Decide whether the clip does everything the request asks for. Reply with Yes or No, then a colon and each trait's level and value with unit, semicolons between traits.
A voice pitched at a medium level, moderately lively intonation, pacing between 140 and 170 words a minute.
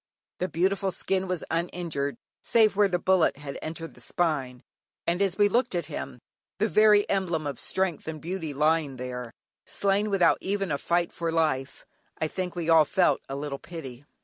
No: medium, 170 Hz; average, 4.4 semitones; average, 180 wpm